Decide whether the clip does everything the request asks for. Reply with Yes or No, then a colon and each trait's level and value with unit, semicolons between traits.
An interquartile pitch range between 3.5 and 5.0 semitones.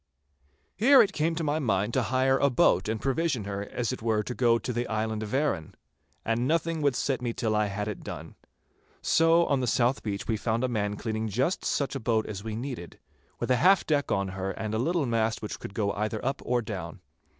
Yes: average, 4.3 semitones